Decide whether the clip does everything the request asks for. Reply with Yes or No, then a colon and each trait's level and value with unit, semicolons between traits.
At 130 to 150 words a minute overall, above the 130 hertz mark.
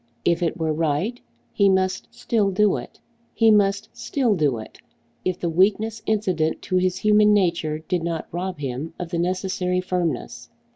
No: average, 165 wpm; medium, 185 Hz